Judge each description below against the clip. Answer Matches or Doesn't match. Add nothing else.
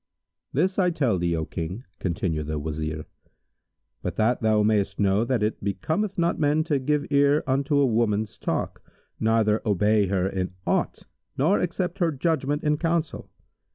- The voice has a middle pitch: Doesn't match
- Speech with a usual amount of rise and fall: Doesn't match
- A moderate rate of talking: Matches